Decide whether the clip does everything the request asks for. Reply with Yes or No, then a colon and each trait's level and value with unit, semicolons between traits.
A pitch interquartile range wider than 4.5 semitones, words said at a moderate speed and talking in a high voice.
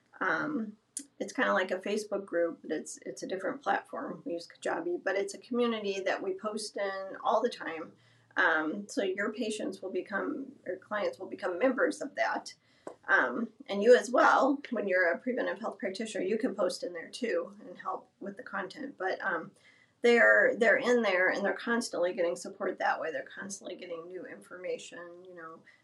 Yes: average, 5.1 semitones; average, 195 wpm; high, 205 Hz